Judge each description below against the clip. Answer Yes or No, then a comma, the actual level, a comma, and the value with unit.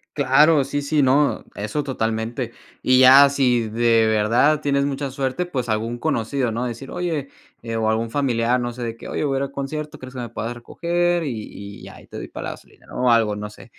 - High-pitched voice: No, low, 130 Hz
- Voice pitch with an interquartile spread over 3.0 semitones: Yes, average, 3.6 semitones